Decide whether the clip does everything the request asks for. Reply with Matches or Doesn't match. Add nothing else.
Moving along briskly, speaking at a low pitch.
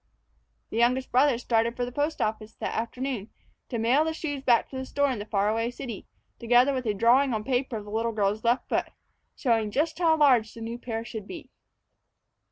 Doesn't match